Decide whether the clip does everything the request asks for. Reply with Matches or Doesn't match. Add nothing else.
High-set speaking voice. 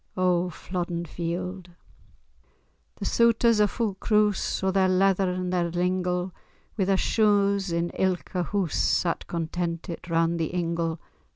Doesn't match